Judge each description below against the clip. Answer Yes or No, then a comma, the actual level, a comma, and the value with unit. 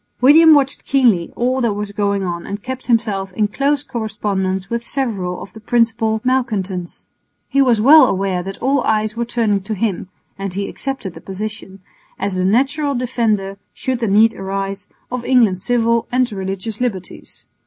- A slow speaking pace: No, average, 170 wpm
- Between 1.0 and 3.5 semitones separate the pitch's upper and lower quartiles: No, average, 4.2 semitones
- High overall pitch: Yes, high, 220 Hz